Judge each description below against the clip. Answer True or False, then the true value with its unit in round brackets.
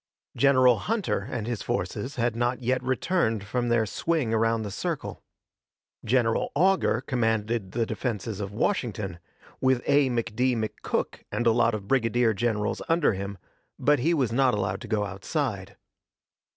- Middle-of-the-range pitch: False (120 Hz)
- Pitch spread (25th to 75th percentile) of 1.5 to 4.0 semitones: True (3.3 semitones)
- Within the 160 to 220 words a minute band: False (150 wpm)